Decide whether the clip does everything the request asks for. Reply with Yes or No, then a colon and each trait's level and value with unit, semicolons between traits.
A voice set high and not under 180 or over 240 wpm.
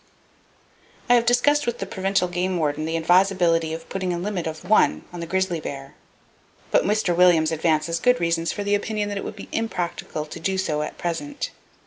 No: medium, 180 Hz; average, 195 wpm